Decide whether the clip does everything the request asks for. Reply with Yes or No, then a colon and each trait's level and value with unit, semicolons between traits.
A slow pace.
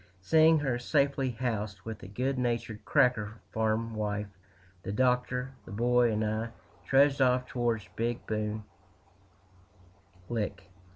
Yes: slow, 125 wpm